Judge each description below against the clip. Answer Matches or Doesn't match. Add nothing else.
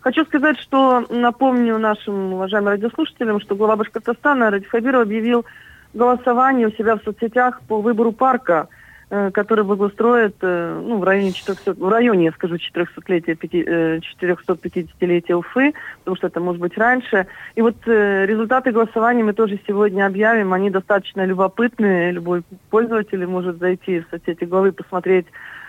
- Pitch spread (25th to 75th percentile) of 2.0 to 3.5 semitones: Doesn't match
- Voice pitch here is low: Doesn't match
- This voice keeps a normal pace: Matches